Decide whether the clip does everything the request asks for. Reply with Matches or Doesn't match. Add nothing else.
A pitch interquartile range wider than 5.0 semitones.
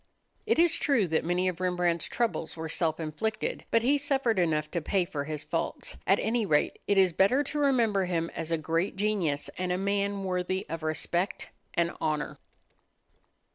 Doesn't match